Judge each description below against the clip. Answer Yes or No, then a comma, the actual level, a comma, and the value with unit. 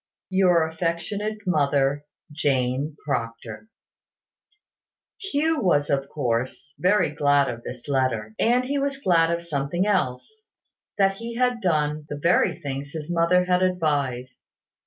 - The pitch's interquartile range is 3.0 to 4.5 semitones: No, average, 5.3 semitones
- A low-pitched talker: No, medium, 160 Hz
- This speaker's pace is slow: Yes, slow, 130 wpm